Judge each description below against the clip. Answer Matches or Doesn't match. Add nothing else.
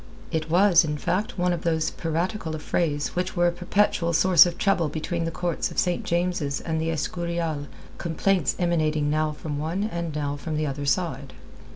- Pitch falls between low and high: Matches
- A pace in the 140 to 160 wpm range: Doesn't match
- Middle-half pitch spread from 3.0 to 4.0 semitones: Doesn't match